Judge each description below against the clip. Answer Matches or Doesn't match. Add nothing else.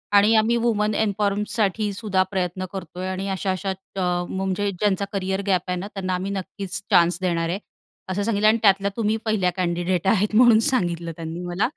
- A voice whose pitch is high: Matches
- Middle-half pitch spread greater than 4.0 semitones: Doesn't match